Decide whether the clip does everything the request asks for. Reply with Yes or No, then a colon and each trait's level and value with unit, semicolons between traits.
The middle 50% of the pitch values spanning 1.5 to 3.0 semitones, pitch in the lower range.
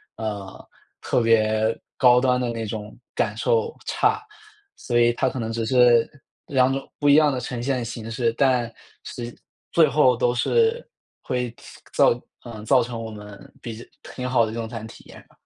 Yes: narrow, 2.5 semitones; low, 120 Hz